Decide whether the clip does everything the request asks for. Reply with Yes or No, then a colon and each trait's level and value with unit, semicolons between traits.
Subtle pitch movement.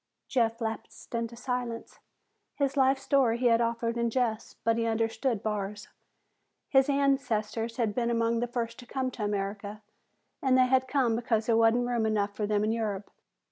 Yes: narrow, 2.1 semitones